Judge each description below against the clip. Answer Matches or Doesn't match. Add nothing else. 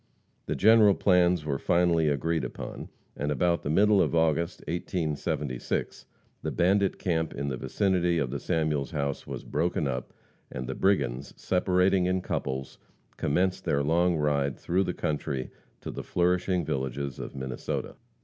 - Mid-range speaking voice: Doesn't match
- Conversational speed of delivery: Matches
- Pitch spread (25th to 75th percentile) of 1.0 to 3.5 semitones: Doesn't match